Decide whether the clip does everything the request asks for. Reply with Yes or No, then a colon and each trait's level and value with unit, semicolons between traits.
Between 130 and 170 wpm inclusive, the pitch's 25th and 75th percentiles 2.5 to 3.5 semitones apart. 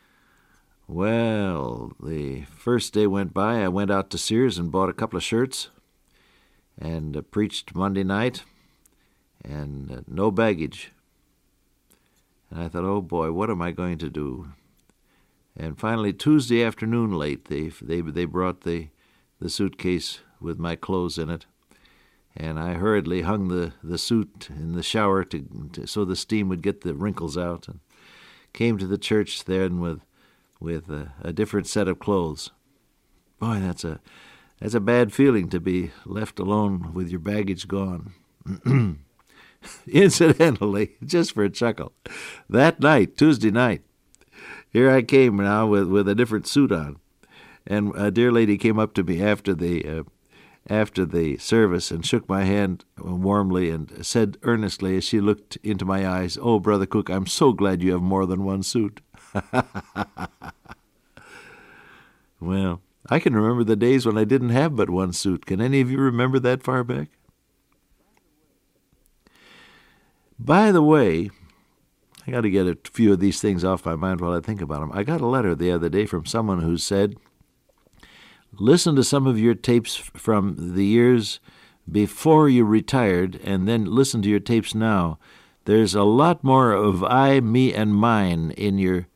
No: average, 165 wpm; average, 4.2 semitones